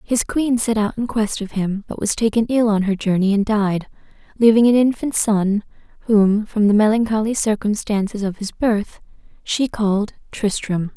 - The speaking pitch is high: Yes, high, 215 Hz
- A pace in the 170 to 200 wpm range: Yes, average, 175 wpm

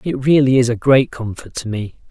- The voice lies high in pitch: No, low, 125 Hz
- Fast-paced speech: Yes, fast, 230 wpm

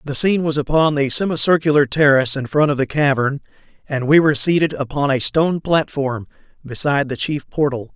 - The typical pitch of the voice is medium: Yes, medium, 145 Hz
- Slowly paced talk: No, average, 180 wpm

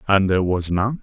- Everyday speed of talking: No, fast, 235 wpm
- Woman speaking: No, male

